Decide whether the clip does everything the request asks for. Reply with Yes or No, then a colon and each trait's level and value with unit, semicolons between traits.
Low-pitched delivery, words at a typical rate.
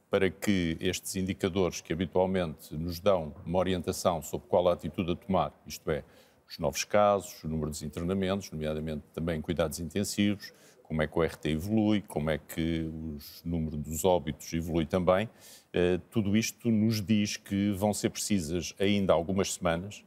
Yes: very low, 90 Hz; average, 165 wpm